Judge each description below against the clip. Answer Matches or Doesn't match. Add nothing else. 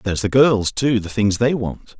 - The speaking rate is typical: Doesn't match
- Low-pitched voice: Matches